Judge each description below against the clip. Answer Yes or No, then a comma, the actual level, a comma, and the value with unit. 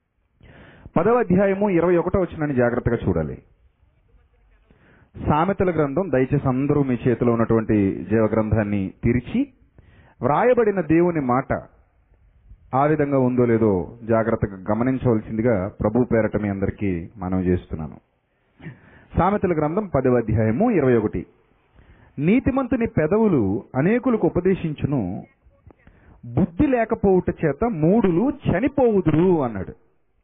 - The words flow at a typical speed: Yes, average, 95 wpm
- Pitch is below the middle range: Yes, low, 125 Hz